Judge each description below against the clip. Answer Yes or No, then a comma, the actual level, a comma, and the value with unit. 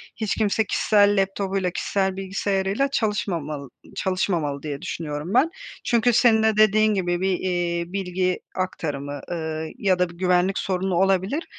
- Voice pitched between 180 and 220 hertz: Yes, high, 190 Hz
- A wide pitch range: No, average, 2.8 semitones